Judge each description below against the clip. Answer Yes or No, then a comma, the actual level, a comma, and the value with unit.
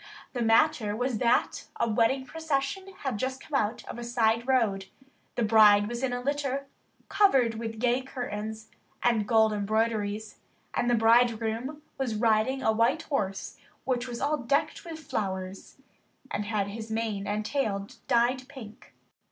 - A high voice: Yes, high, 235 Hz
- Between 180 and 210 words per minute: No, average, 155 wpm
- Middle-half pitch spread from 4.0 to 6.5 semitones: No, average, 3.4 semitones